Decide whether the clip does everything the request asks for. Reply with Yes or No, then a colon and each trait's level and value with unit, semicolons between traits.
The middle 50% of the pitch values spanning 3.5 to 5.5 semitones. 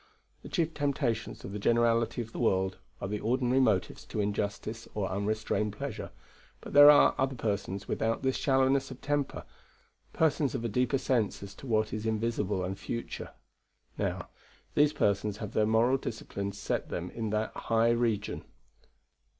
Yes: average, 4.0 semitones